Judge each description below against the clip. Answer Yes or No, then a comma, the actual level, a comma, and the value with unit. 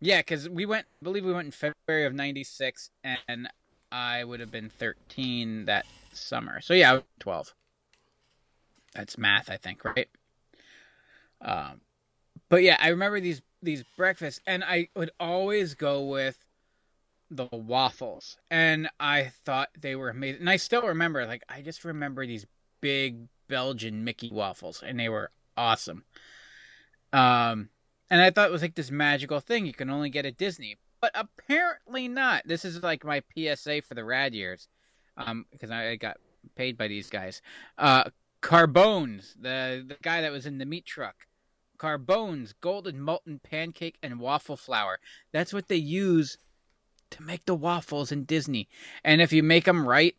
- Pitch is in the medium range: Yes, medium, 150 Hz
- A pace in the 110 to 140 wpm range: No, average, 165 wpm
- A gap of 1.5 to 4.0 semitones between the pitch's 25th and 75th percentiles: No, average, 5.2 semitones